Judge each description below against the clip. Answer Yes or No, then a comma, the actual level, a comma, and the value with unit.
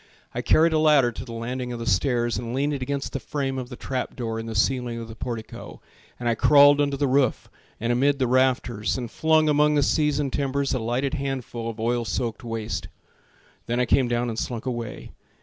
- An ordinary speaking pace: No, fast, 220 wpm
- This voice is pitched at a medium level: No, low, 125 Hz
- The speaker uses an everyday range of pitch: Yes, average, 3.1 semitones